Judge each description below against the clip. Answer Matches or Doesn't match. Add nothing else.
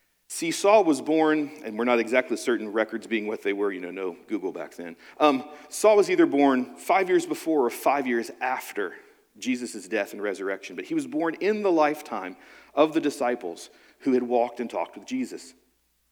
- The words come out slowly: Doesn't match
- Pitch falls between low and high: Matches